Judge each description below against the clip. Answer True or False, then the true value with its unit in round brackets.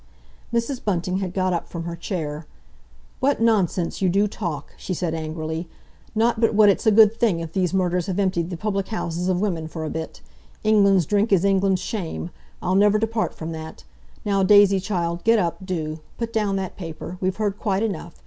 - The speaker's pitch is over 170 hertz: True (190 Hz)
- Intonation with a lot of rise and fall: False (3.6 semitones)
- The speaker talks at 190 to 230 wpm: True (195 wpm)